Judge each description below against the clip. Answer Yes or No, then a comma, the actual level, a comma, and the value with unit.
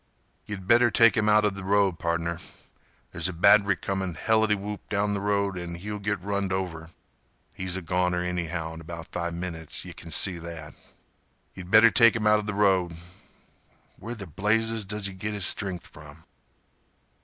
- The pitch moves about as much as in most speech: Yes, average, 3.4 semitones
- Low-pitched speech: Yes, very low, 95 Hz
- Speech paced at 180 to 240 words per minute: No, average, 165 wpm